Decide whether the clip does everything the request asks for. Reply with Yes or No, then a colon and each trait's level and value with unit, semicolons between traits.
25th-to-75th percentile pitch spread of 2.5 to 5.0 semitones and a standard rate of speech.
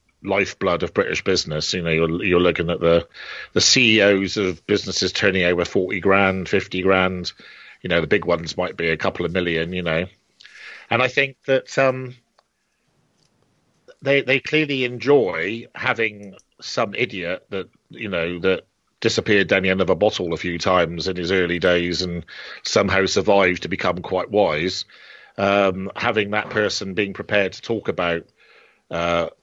Yes: average, 3.3 semitones; average, 165 wpm